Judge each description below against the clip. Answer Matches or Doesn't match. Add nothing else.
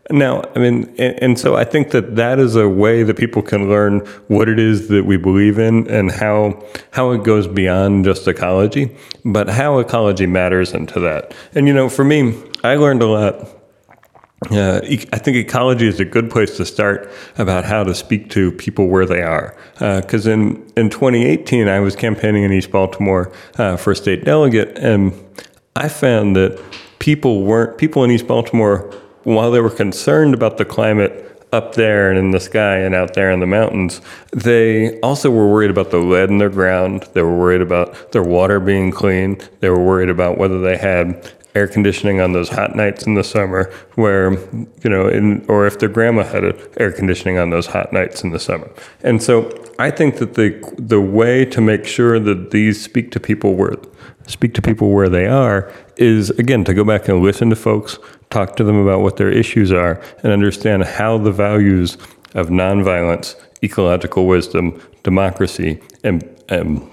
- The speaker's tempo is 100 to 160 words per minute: Doesn't match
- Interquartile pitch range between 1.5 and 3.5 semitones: Matches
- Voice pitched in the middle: Doesn't match